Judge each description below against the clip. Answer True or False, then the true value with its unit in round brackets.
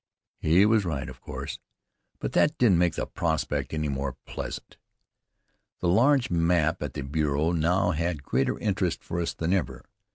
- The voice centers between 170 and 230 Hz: False (85 Hz)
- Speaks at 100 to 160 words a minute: False (170 wpm)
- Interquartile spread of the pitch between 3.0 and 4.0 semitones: True (3.4 semitones)